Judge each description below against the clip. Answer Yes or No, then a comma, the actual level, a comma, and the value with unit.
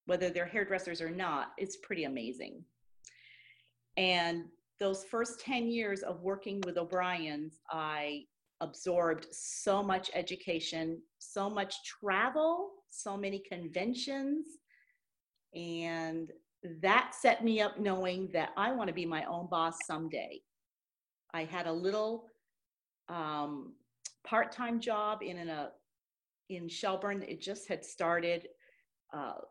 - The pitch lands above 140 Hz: Yes, medium, 185 Hz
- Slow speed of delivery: Yes, slow, 120 wpm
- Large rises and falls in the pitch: No, average, 3.9 semitones